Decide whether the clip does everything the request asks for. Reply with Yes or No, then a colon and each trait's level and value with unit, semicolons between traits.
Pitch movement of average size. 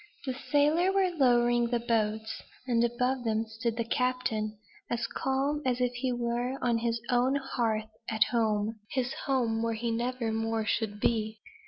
No: narrow, 2.3 semitones